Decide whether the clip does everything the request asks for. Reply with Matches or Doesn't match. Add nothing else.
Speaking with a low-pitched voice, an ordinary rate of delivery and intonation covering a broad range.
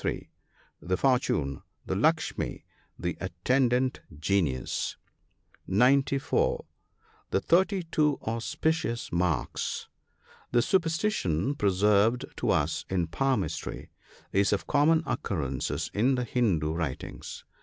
Doesn't match